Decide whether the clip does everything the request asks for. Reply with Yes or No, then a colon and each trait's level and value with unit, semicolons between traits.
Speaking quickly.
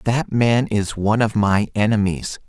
No: average, 170 wpm